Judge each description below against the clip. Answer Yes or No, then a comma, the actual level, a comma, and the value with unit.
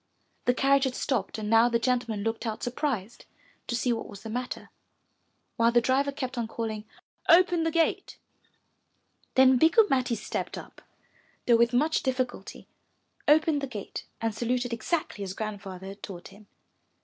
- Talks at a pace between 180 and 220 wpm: No, average, 160 wpm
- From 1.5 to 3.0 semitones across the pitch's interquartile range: No, average, 3.4 semitones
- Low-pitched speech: No, high, 240 Hz